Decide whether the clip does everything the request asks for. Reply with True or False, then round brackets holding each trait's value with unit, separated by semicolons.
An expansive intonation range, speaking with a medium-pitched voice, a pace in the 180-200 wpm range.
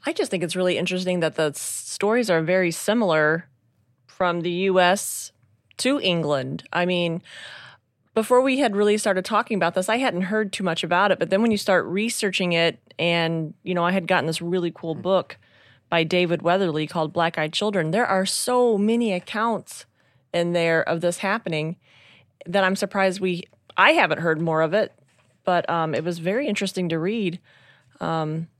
False (3.4 semitones; 175 Hz; 185 wpm)